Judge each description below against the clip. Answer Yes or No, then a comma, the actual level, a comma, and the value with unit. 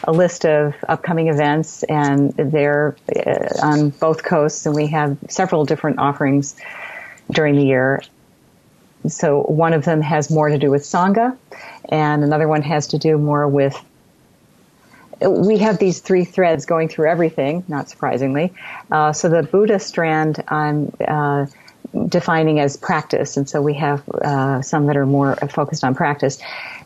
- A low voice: No, medium, 150 Hz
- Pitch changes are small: Yes, narrow, 2.3 semitones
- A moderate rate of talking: Yes, average, 155 wpm